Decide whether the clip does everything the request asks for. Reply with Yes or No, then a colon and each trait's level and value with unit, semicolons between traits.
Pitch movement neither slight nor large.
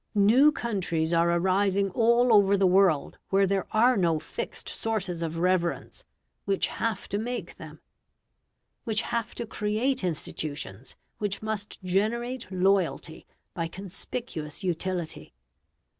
Yes: average, 4.3 semitones